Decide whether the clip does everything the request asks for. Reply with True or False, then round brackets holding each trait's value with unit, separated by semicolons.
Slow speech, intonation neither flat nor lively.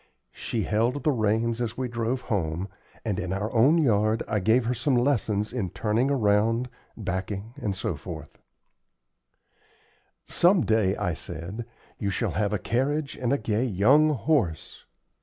False (145 wpm; 3.7 semitones)